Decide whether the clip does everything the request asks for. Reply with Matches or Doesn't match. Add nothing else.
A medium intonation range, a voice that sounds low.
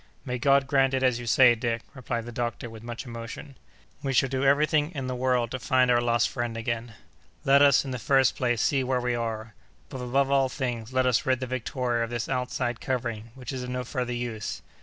Doesn't match